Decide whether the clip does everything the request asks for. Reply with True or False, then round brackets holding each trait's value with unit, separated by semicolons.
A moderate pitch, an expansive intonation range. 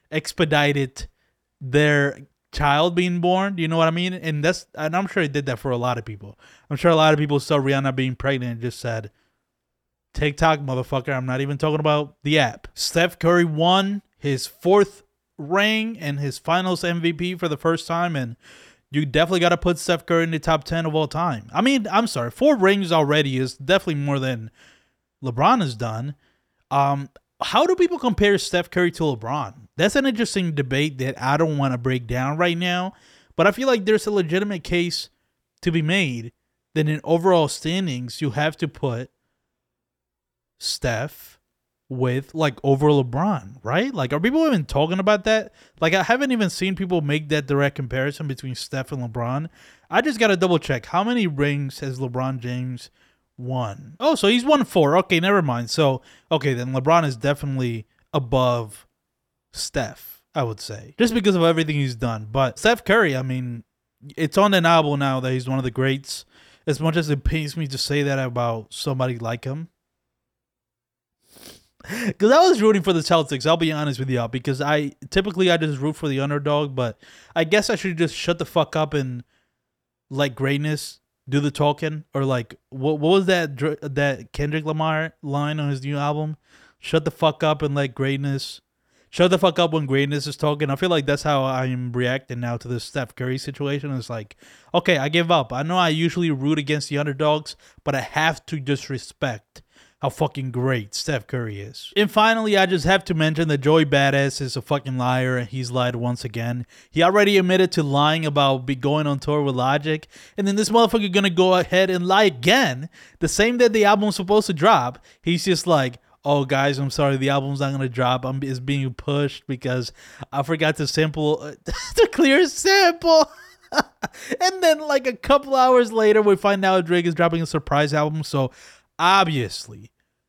False (150 Hz; 4.8 semitones)